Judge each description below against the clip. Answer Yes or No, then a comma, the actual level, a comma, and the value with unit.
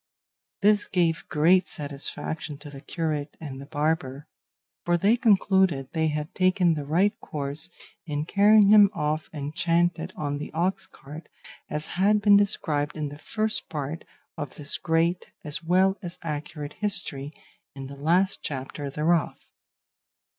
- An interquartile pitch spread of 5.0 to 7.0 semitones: No, average, 4.0 semitones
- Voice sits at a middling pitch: Yes, medium, 160 Hz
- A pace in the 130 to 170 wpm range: Yes, average, 145 wpm